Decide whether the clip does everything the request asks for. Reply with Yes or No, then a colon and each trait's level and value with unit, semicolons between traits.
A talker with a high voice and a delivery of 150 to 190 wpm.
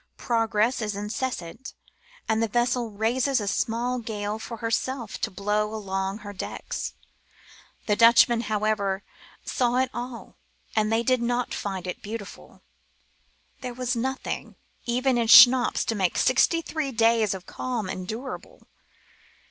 No: high, 230 Hz; average, 140 wpm